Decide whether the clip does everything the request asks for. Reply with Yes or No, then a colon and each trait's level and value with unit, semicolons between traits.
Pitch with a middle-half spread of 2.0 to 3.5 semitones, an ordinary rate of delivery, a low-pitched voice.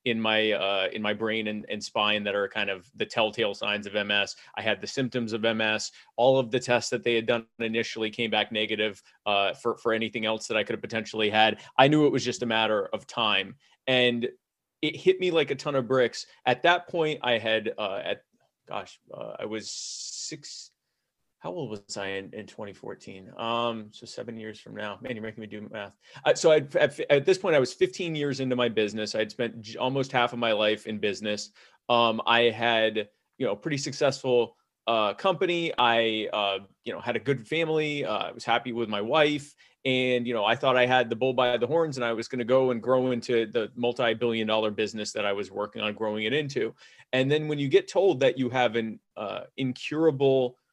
No: average, 3.2 semitones; fast, 220 wpm; low, 120 Hz